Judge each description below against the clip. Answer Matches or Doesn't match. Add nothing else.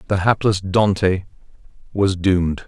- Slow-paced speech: Matches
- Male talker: Matches